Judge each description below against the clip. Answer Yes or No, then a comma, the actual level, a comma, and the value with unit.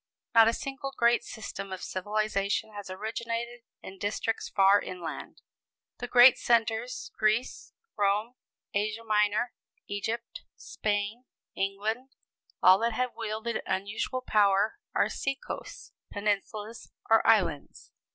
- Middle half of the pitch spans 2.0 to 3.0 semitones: Yes, narrow, 2.5 semitones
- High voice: Yes, high, 215 Hz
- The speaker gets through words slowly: Yes, slow, 115 wpm